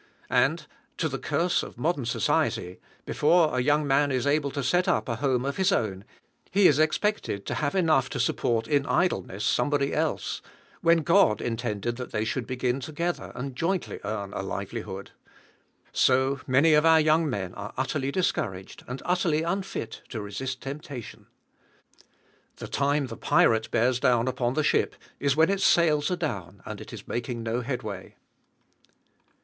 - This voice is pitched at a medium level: No, low, 130 Hz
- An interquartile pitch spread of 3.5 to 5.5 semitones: Yes, average, 5.2 semitones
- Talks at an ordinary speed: Yes, average, 165 wpm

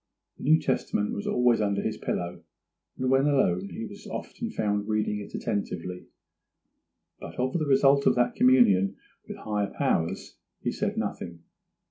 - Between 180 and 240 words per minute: No, average, 155 wpm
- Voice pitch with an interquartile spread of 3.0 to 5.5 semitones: Yes, average, 4.6 semitones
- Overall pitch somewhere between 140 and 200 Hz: No, low, 105 Hz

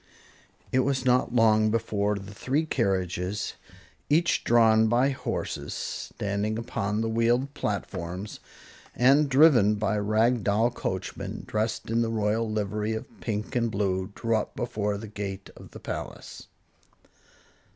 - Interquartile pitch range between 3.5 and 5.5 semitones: No, narrow, 2.6 semitones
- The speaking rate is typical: No, slow, 130 wpm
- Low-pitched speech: Yes, low, 110 Hz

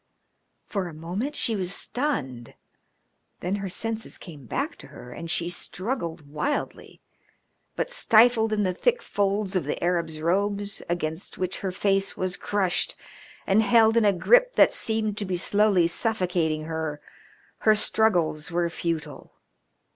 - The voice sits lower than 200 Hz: Yes, high, 190 Hz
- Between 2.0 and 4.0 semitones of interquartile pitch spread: No, average, 4.4 semitones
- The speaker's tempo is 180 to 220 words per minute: No, average, 145 wpm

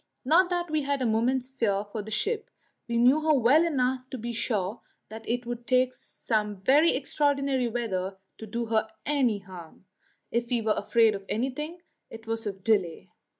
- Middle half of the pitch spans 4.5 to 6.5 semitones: No, average, 3.8 semitones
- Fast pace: No, average, 185 wpm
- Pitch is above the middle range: Yes, high, 235 Hz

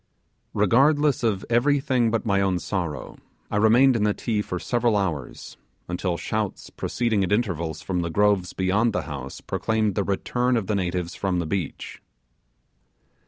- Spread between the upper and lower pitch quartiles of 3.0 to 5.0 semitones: Yes, average, 4.5 semitones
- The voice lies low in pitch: Yes, low, 105 Hz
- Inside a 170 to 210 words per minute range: No, average, 160 wpm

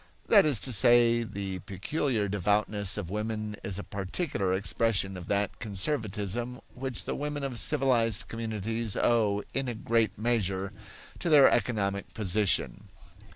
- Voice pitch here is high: No, low, 110 Hz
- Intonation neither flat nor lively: Yes, average, 3.2 semitones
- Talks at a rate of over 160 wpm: No, slow, 135 wpm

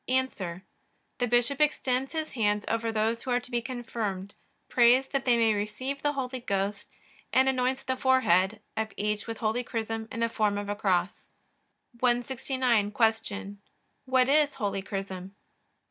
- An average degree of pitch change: Yes, average, 3.7 semitones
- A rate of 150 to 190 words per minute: Yes, average, 160 wpm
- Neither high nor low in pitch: No, high, 230 Hz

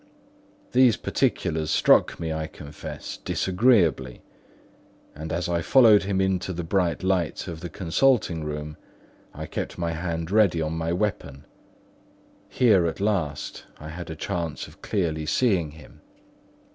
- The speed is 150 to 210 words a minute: No, average, 140 wpm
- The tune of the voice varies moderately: Yes, average, 3.4 semitones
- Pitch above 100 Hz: No, very low, 85 Hz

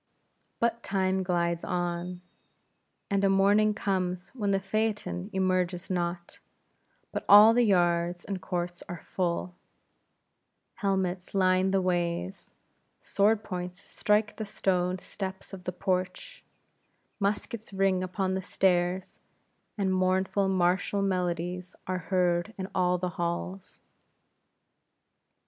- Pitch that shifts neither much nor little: No, narrow, 1.7 semitones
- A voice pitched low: No, medium, 185 Hz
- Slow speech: Yes, slow, 115 wpm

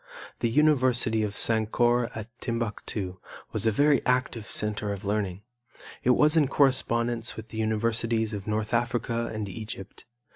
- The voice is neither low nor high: No, low, 115 Hz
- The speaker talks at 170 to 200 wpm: No, average, 145 wpm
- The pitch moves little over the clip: Yes, narrow, 2.2 semitones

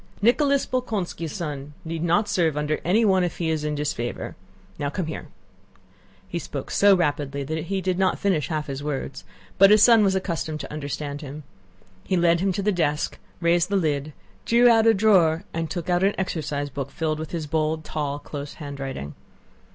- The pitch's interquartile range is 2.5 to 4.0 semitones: No, average, 4.5 semitones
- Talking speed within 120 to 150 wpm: No, average, 190 wpm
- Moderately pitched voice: Yes, medium, 160 Hz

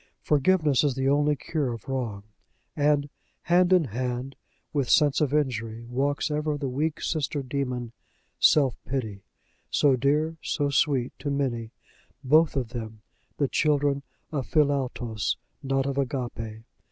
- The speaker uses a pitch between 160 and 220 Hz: No, low, 135 Hz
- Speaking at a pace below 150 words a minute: Yes, average, 140 wpm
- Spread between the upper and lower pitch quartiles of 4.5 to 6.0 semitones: No, average, 3.1 semitones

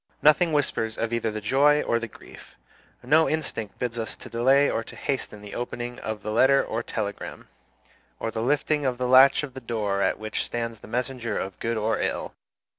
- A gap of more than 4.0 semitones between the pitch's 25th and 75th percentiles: No, average, 3.4 semitones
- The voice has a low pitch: Yes, low, 120 Hz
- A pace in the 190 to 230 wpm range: Yes, average, 200 wpm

